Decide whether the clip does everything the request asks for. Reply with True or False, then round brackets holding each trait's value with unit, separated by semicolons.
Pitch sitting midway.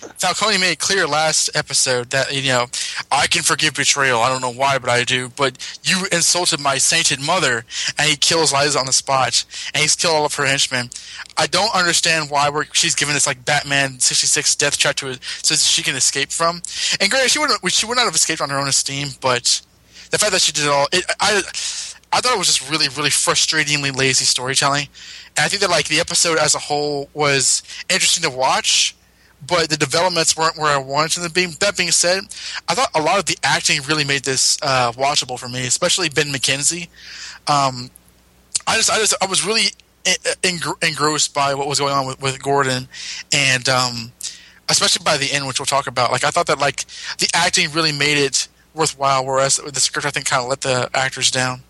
True (145 Hz)